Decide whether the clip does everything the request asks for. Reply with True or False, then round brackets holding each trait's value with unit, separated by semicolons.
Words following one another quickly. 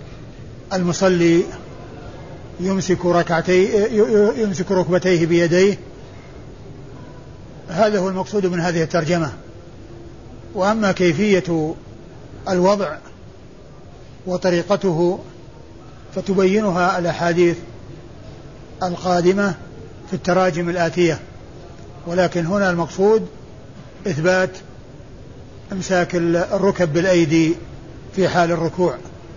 False (65 wpm)